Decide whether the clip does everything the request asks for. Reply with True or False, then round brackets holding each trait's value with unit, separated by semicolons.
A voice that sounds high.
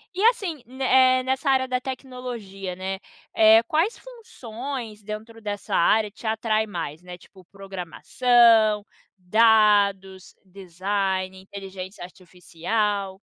True (210 Hz)